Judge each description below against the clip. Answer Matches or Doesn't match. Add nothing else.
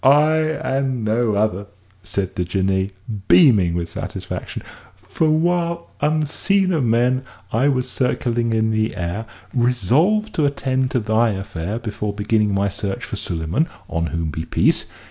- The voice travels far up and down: Matches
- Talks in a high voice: Doesn't match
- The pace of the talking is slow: Doesn't match